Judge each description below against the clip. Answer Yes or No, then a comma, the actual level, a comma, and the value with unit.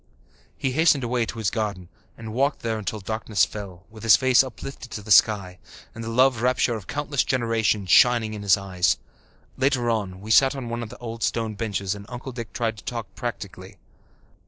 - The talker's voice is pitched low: Yes, low, 115 Hz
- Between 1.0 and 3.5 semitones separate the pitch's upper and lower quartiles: Yes, average, 3.0 semitones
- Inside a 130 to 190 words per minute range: No, average, 200 wpm